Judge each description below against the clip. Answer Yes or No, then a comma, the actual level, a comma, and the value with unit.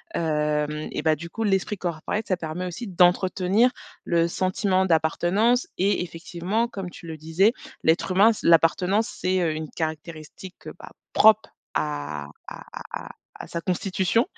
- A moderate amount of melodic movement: Yes, average, 3.5 semitones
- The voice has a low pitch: No, medium, 180 Hz